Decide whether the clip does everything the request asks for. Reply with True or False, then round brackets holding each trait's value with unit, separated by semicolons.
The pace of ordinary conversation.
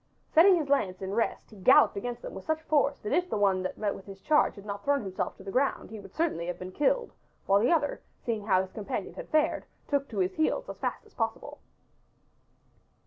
False (230 wpm)